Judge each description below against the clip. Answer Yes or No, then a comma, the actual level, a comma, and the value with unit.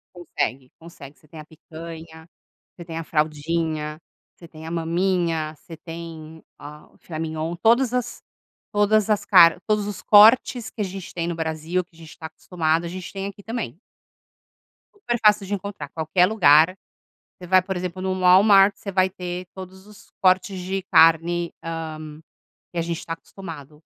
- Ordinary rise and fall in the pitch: Yes, average, 3.1 semitones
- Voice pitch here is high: No, medium, 170 Hz